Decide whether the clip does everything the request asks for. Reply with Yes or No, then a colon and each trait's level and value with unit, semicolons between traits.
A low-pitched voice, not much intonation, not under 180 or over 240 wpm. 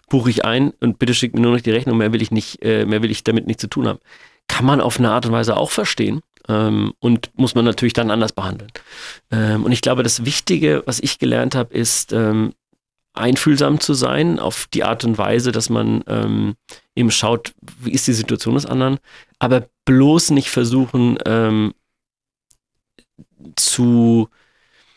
Yes: low, 115 Hz; narrow, 2.3 semitones; average, 185 wpm